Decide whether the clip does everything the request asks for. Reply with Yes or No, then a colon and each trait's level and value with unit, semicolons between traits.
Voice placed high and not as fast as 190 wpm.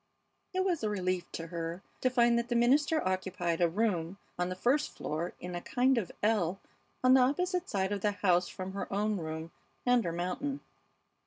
No: high, 200 Hz; average, 195 wpm